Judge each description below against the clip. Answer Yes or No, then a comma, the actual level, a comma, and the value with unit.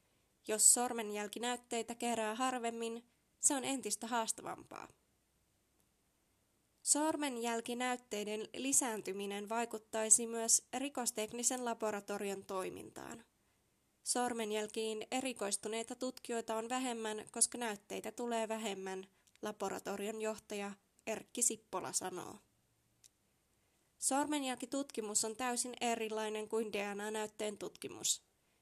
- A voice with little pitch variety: Yes, narrow, 2.3 semitones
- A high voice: Yes, high, 225 Hz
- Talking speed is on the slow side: Yes, slow, 75 wpm